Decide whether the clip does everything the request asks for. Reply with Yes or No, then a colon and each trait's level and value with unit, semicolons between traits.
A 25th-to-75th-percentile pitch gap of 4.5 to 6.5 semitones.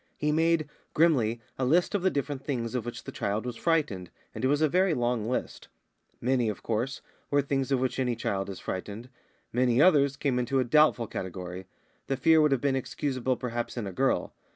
No: average, 3.7 semitones